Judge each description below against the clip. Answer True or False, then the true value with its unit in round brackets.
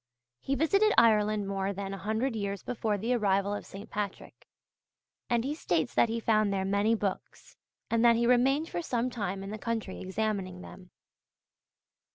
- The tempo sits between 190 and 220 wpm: False (175 wpm)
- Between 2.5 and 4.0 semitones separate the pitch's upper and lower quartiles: True (3.1 semitones)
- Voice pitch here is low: False (215 Hz)